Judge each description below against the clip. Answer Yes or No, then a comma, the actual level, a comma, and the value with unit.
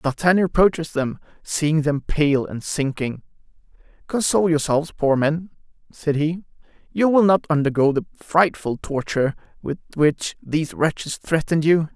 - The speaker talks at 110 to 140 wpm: Yes, slow, 135 wpm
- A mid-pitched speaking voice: Yes, medium, 155 Hz